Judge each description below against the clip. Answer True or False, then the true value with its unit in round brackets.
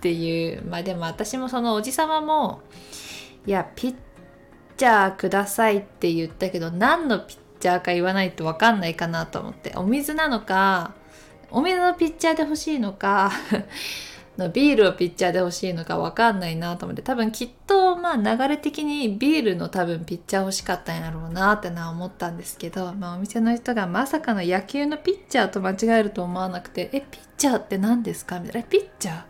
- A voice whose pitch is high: True (205 Hz)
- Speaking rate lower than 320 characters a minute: False (405 characters per minute)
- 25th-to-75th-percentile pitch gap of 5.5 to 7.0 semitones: True (6.0 semitones)